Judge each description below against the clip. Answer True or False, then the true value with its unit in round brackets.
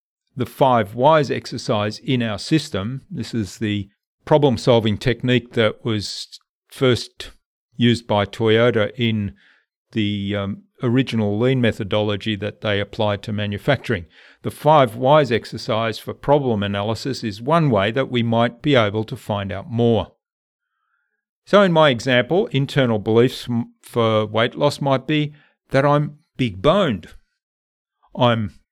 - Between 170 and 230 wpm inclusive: False (135 wpm)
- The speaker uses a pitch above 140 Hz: False (115 Hz)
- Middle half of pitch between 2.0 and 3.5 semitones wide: False (3.9 semitones)